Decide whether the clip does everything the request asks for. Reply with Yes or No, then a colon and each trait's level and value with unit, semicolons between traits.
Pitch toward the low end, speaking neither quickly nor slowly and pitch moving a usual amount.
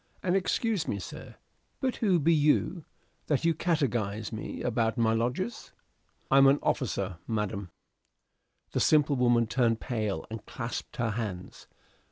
No: low, 120 Hz; average, 150 wpm; wide, 5.9 semitones